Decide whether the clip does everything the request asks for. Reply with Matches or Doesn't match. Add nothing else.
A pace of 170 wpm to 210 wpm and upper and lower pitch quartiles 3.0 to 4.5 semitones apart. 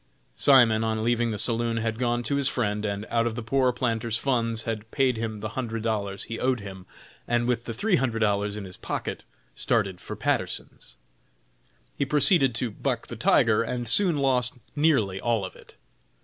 Doesn't match